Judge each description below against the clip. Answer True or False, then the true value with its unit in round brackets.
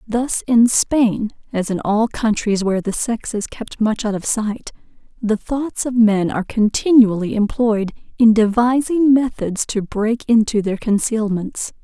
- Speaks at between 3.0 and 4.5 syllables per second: True (4.2 syllables/s)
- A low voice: False (220 Hz)